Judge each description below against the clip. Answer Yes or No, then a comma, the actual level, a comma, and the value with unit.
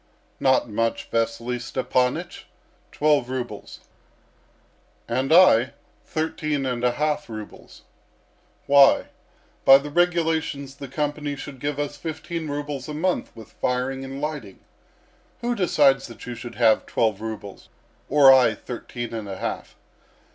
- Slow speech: Yes, slow, 130 wpm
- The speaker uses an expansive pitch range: No, average, 3.7 semitones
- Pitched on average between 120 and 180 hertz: Yes, low, 135 Hz